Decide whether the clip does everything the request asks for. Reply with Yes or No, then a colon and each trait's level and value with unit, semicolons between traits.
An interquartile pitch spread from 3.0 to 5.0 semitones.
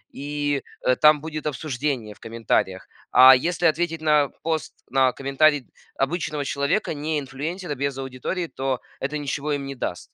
No: narrow, 2.6 semitones